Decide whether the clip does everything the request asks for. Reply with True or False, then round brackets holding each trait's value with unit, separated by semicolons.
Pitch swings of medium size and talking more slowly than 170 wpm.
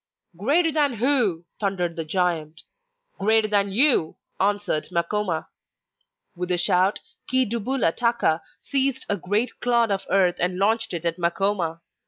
True (5.0 semitones; 140 wpm)